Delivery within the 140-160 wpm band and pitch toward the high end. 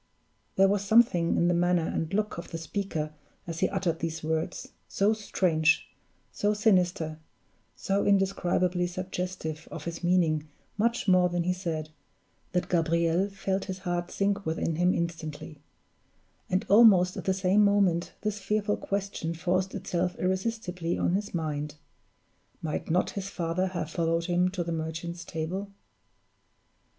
No: average, 145 wpm; medium, 180 Hz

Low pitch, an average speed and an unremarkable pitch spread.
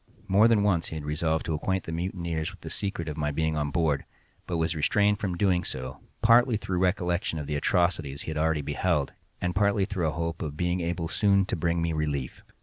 No: very low, 85 Hz; fast, 225 wpm; average, 3.3 semitones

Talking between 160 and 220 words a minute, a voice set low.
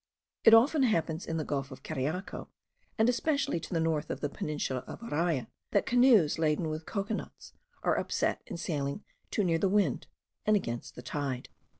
No: average, 185 wpm; medium, 165 Hz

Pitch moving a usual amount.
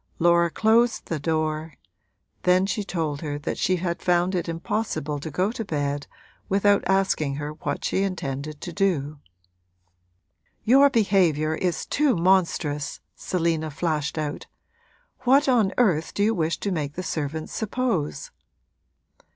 Yes: average, 4.4 semitones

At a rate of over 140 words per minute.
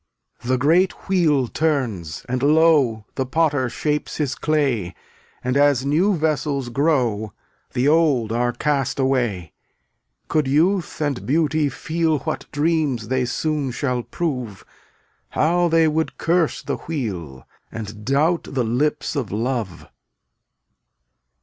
No: slow, 135 wpm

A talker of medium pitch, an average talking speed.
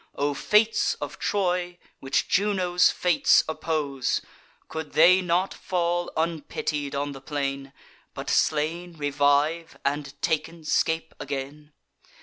No: medium, 155 Hz; slow, 115 wpm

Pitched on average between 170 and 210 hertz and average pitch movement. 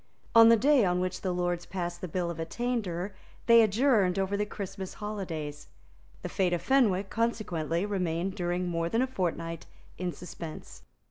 Yes: medium, 185 Hz; average, 3.5 semitones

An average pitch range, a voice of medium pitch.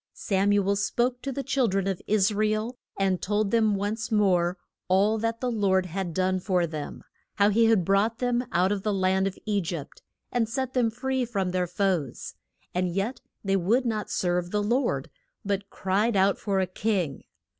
No: average, 3.1 semitones; high, 200 Hz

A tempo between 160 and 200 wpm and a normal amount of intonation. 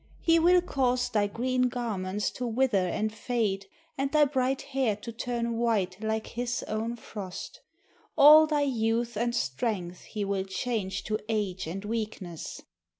No: average, 150 wpm; average, 3.7 semitones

